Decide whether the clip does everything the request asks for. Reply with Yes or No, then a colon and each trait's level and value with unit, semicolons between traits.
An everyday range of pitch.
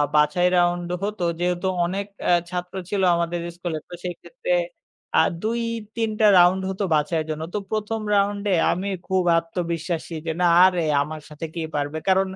Yes: average, 3.1 semitones